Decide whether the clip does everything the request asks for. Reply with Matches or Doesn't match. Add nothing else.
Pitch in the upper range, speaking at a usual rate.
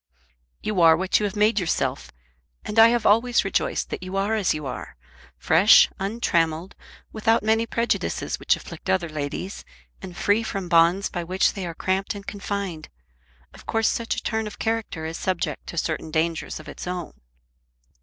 Matches